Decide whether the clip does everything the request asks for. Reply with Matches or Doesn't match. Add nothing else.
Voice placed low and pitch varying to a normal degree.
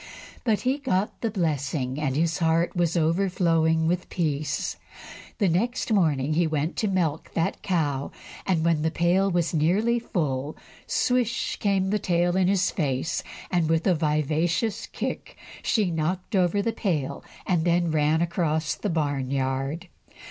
Doesn't match